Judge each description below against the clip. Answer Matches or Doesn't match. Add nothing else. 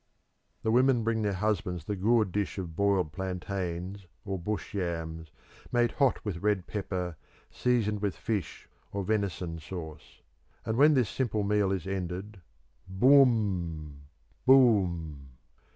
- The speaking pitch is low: Matches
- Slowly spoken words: Matches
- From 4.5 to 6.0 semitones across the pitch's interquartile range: Doesn't match